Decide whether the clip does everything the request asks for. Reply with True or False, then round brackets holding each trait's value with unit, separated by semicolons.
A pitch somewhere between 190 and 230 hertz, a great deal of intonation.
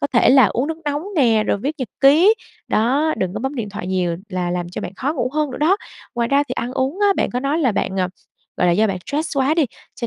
False (255 Hz; 6.2 semitones)